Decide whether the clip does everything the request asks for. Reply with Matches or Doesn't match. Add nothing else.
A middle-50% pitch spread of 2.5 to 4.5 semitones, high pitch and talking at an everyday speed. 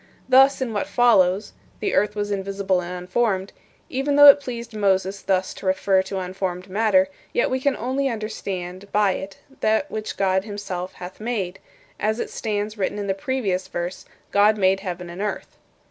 Matches